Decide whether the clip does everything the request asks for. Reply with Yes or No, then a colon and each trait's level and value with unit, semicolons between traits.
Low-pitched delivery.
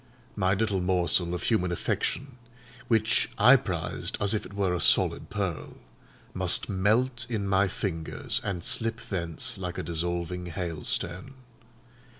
Yes: very low, 95 Hz